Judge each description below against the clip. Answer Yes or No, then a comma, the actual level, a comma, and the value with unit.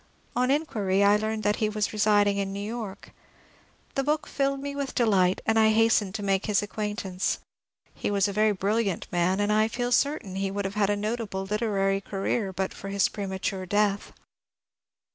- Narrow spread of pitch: Yes, narrow, 2.1 semitones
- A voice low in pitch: No, high, 205 Hz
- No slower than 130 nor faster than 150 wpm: No, average, 200 wpm